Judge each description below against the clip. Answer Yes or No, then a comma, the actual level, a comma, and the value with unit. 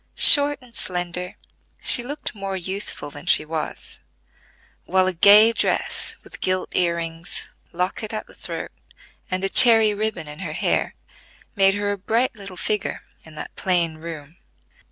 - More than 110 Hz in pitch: Yes, medium, 185 Hz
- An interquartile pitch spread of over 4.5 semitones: No, average, 3.8 semitones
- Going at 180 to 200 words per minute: No, average, 155 wpm